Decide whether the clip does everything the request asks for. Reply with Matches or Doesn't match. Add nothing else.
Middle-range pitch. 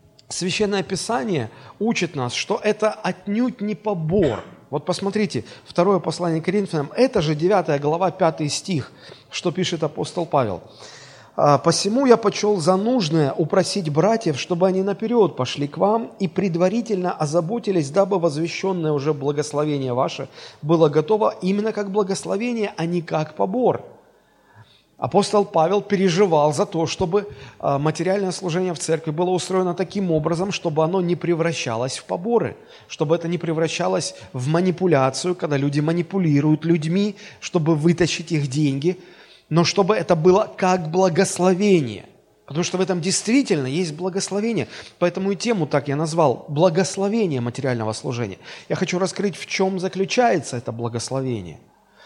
Matches